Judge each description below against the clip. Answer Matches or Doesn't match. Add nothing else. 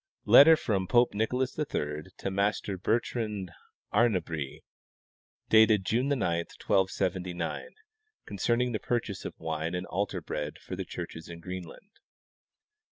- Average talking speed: Doesn't match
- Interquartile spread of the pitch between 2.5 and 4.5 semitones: Doesn't match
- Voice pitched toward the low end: Matches